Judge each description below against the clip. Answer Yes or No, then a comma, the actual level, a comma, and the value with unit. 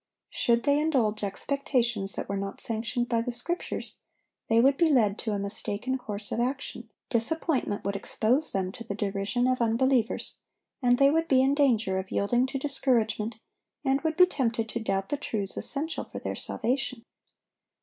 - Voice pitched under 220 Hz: No, high, 240 Hz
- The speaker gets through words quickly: No, average, 175 wpm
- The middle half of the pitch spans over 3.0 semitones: Yes, average, 4.3 semitones